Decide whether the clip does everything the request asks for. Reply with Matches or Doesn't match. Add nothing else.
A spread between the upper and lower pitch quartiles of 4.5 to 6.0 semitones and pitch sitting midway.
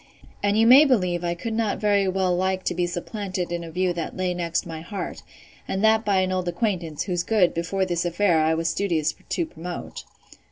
Doesn't match